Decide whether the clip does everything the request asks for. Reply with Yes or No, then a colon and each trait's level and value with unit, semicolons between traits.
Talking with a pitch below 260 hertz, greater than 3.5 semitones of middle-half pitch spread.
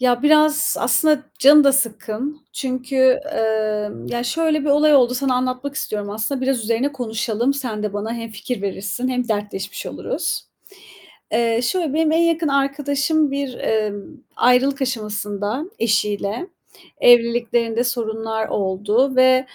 Yes: very high, 250 Hz; average, 4.2 semitones